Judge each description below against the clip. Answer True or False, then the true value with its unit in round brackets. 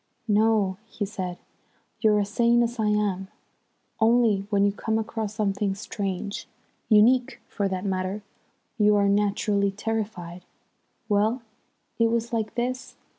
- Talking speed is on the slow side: True (130 wpm)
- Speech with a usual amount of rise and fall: False (2.1 semitones)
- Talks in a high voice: True (210 Hz)